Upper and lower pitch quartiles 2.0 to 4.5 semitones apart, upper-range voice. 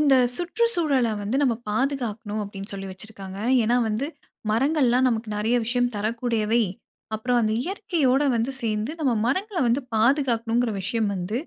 Yes: average, 4.0 semitones; high, 235 Hz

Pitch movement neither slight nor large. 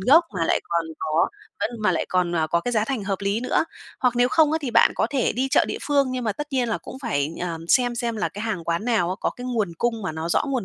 No: wide, 5.9 semitones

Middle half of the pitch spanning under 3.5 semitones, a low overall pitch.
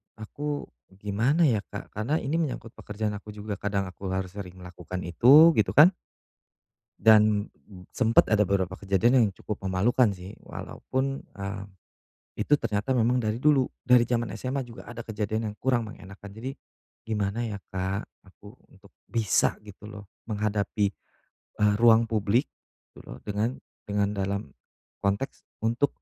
Yes: average, 3.1 semitones; low, 105 Hz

